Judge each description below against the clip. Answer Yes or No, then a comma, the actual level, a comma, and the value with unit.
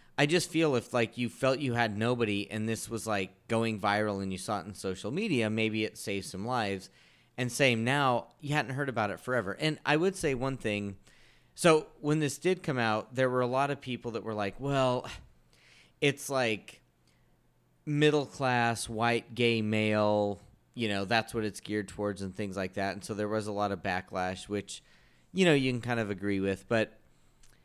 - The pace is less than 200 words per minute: No, fast, 205 wpm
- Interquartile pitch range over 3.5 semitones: Yes, average, 4.1 semitones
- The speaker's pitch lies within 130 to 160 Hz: No, low, 110 Hz